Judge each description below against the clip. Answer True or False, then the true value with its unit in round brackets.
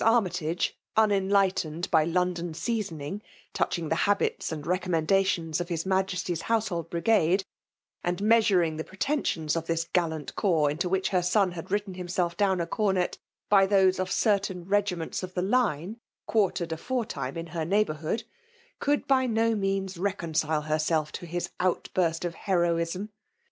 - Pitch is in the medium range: True (180 Hz)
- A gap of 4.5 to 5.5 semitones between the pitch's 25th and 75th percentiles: False (3.2 semitones)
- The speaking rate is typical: True (150 wpm)